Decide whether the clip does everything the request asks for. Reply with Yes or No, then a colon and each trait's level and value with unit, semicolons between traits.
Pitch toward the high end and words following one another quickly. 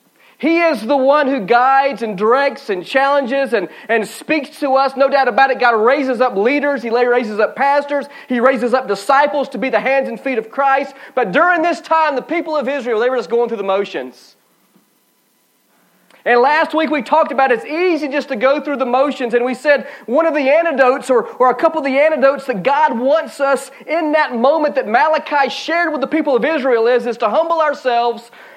Yes: very high, 275 Hz; fast, 215 wpm